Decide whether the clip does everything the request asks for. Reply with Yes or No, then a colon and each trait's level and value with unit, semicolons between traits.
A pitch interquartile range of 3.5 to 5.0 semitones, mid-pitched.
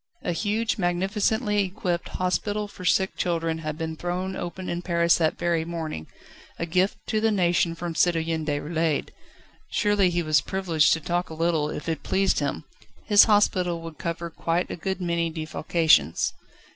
No: average, 2.7 semitones; medium, 170 Hz